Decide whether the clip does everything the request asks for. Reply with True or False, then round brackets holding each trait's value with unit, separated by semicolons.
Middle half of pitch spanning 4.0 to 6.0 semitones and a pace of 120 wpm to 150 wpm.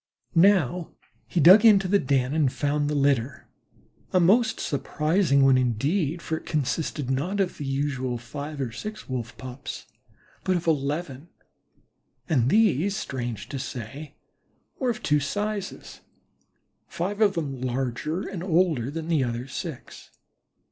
True (5.4 semitones; 140 wpm)